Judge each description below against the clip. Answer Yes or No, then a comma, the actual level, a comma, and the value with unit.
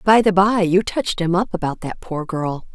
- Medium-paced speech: No, fast, 240 wpm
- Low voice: No, medium, 185 Hz